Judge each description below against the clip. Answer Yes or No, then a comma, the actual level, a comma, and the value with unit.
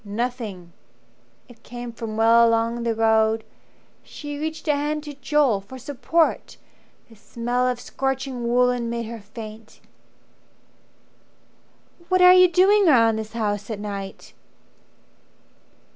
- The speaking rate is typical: No, slow, 125 wpm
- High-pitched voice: Yes, high, 235 Hz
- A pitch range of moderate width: Yes, average, 4.0 semitones